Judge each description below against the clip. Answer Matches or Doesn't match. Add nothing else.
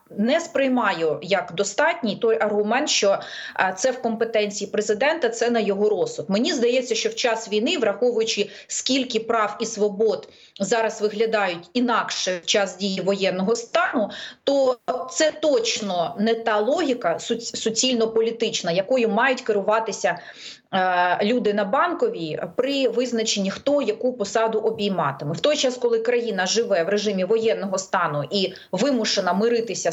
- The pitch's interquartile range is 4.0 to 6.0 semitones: Doesn't match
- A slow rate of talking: Doesn't match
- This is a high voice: Matches